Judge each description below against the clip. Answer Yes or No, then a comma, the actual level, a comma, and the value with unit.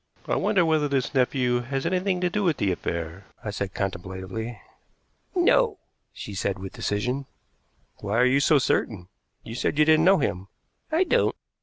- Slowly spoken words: No, average, 170 wpm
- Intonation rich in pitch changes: Yes, wide, 8.2 semitones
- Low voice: Yes, low, 125 Hz